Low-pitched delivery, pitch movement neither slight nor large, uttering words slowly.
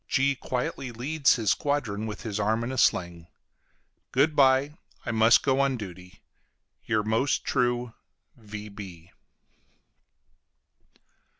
Yes: low, 115 Hz; average, 4.2 semitones; slow, 115 wpm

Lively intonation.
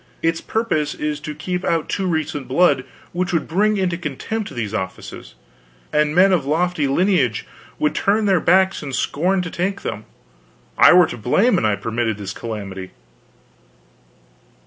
Yes: wide, 6.2 semitones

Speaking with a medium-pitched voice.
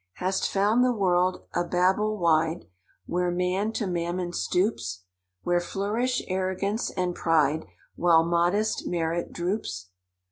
Yes: medium, 180 Hz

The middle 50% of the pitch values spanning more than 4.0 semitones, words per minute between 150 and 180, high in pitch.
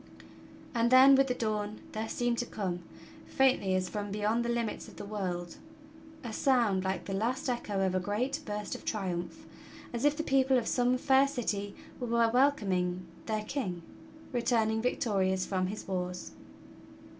Yes: average, 4.5 semitones; average, 165 wpm; high, 215 Hz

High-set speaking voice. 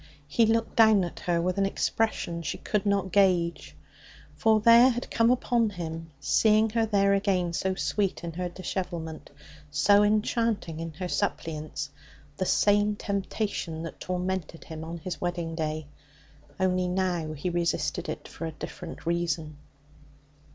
No: medium, 180 Hz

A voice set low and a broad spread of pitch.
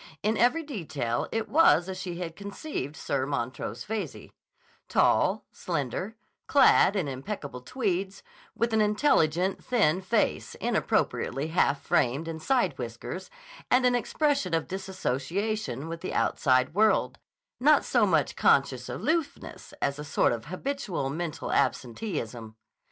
No: medium, 175 Hz; wide, 7.7 semitones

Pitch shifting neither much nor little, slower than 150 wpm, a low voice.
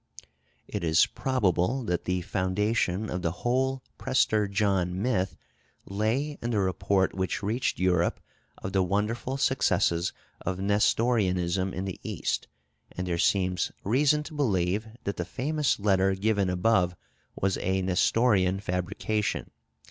Yes: average, 3.8 semitones; slow, 135 wpm; low, 100 Hz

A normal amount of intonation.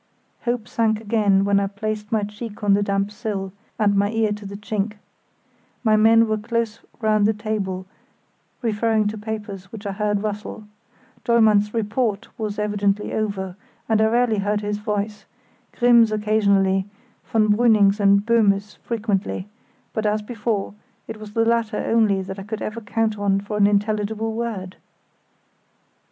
No: narrow, 1.5 semitones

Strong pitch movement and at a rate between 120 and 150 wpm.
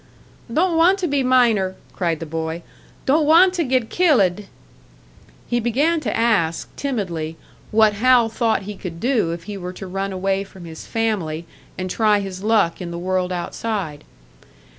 No: wide, 5.7 semitones; average, 170 wpm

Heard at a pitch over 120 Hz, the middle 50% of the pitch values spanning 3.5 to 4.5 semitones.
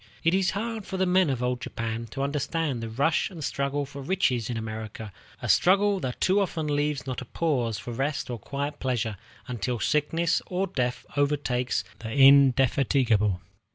No: medium, 140 Hz; average, 5.0 semitones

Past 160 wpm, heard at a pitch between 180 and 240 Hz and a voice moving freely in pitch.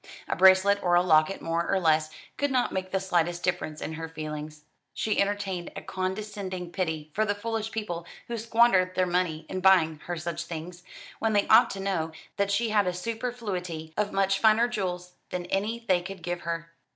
No: average, 195 wpm; medium, 185 Hz; average, 3.2 semitones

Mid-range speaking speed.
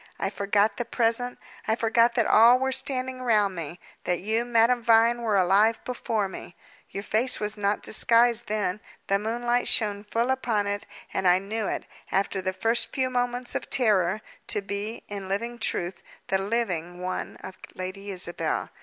Yes: average, 170 wpm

